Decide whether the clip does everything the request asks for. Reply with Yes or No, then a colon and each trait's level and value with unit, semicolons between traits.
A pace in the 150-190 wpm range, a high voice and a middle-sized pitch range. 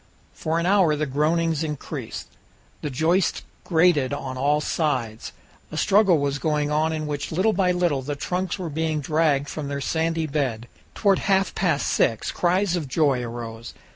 No: average, 170 wpm; medium, 155 Hz; average, 3.3 semitones